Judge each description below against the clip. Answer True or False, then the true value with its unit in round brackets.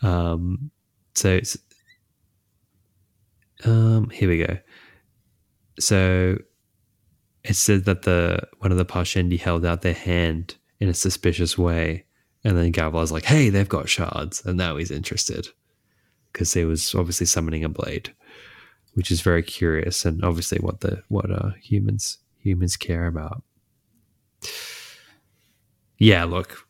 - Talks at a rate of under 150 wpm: True (135 wpm)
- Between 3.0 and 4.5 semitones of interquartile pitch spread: True (3.3 semitones)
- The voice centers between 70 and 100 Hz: True (95 Hz)